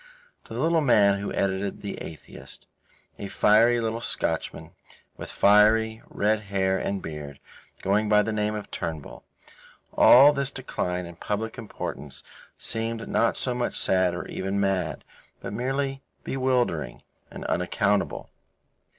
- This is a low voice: Yes, low, 105 Hz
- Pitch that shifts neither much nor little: Yes, average, 3.3 semitones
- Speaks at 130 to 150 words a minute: Yes, slow, 135 wpm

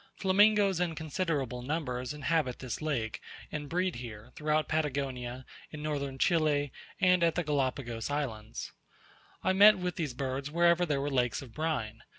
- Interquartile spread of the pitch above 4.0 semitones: Yes, average, 4.5 semitones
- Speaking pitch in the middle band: Yes, medium, 145 Hz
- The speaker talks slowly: No, average, 155 wpm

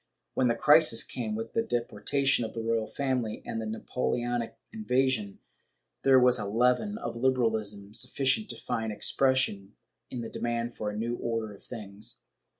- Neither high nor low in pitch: No, low, 120 Hz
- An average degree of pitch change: Yes, average, 3.0 semitones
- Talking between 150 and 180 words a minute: Yes, average, 160 wpm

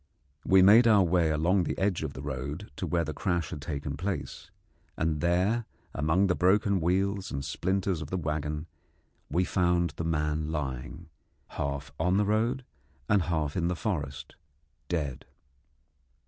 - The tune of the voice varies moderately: Yes, average, 4.1 semitones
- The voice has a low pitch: Yes, very low, 85 Hz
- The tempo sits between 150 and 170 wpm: Yes, average, 160 wpm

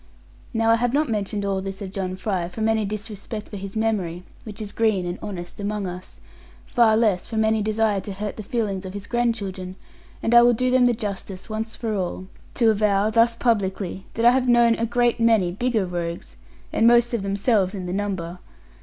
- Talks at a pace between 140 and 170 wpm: No, fast, 205 wpm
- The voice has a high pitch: Yes, high, 210 Hz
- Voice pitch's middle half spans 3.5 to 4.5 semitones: No, average, 3.1 semitones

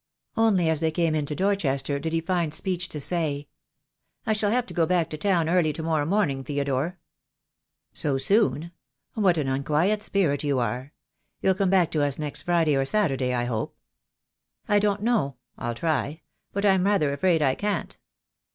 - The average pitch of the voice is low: No, medium, 160 Hz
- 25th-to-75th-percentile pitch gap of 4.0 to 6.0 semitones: Yes, average, 5.1 semitones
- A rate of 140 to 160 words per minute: No, average, 185 wpm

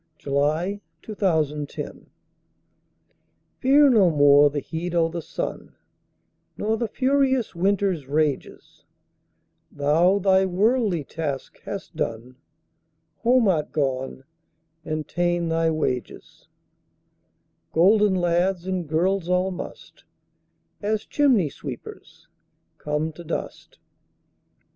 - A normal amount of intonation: Yes, average, 4.9 semitones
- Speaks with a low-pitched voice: No, medium, 175 Hz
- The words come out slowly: Yes, slow, 90 wpm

